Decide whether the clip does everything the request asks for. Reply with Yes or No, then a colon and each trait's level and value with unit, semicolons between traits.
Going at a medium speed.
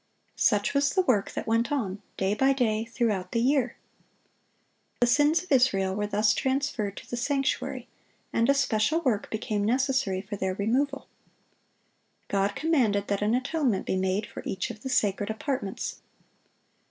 Yes: average, 160 wpm